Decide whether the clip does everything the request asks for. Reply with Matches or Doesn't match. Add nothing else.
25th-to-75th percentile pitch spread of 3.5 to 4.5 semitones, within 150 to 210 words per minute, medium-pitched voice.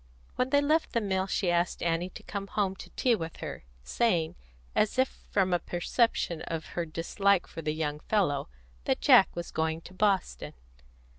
Matches